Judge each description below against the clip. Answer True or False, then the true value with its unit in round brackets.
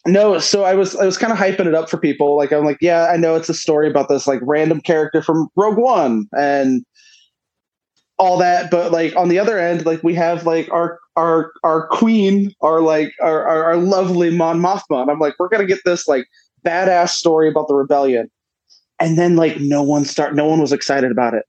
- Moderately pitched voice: True (165 Hz)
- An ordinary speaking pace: False (220 wpm)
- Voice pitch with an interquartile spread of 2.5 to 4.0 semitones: True (2.9 semitones)